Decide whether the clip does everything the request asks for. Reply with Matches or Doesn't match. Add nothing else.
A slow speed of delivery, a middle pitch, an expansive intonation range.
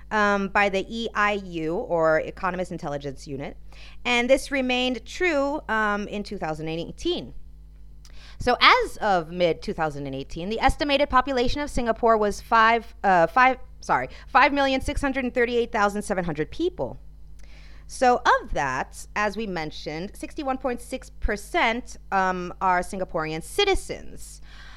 Doesn't match